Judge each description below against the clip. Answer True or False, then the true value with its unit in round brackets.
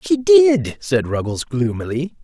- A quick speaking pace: False (135 wpm)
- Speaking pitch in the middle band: True (145 Hz)